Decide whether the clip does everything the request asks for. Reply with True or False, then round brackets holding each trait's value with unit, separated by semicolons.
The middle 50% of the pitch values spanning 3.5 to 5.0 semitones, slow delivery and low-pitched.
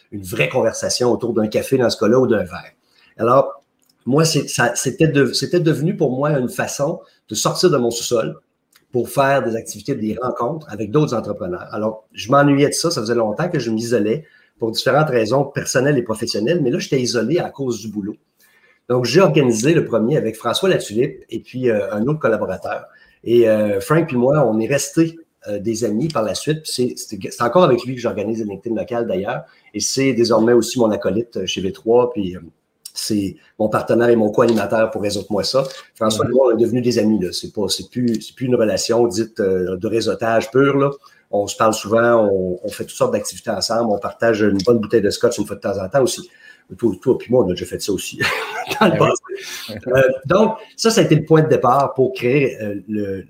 False (4.3 semitones; 210 wpm; 120 Hz)